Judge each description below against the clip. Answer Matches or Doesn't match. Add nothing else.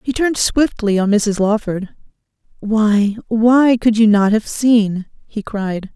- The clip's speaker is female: Matches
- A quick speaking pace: Doesn't match